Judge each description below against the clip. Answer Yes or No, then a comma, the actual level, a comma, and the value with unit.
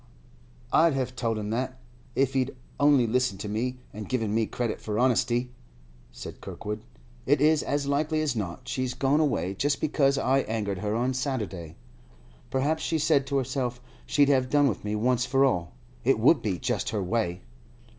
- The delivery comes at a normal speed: Yes, average, 180 wpm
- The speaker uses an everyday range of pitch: Yes, average, 4.2 semitones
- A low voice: Yes, low, 125 Hz